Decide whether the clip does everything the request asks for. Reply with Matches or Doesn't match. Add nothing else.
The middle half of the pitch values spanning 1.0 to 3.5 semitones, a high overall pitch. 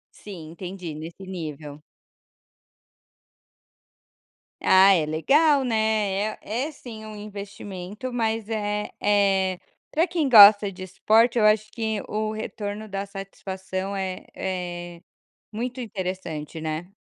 Matches